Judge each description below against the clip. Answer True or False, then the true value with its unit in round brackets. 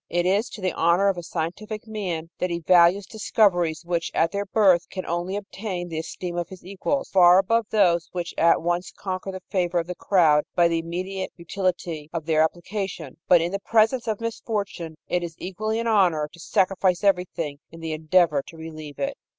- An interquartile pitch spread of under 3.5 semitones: True (3.0 semitones)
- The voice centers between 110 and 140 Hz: False (180 Hz)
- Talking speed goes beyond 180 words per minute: True (200 wpm)